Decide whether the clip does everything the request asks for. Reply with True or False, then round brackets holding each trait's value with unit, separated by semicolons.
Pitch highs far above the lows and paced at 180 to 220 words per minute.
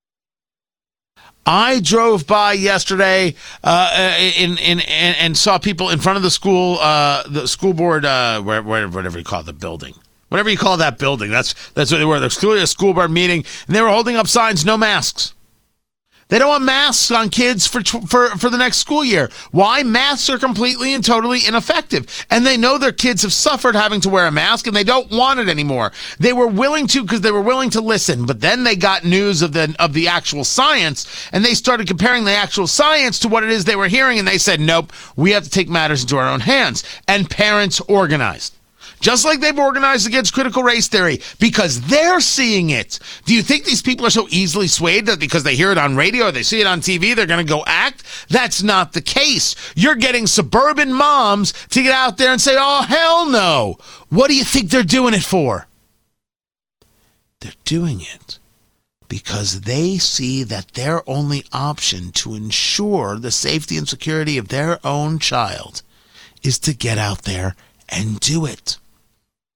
True (7.9 semitones; 205 wpm)